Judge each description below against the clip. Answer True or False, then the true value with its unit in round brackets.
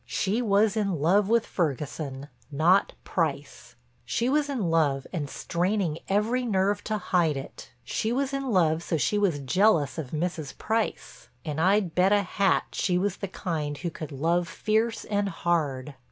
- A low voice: False (180 Hz)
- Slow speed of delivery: False (165 wpm)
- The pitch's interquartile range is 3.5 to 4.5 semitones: False (4.9 semitones)